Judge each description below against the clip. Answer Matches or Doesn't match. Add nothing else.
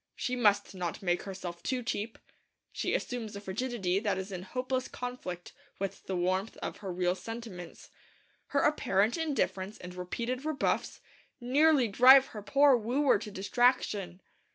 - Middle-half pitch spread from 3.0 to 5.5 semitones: Matches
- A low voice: Doesn't match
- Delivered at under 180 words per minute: Matches